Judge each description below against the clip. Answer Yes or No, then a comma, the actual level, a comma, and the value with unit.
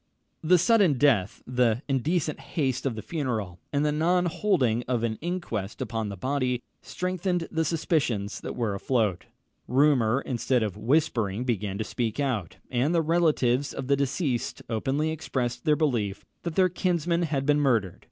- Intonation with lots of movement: Yes, wide, 5.7 semitones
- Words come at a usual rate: Yes, average, 160 wpm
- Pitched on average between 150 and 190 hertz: No, low, 135 Hz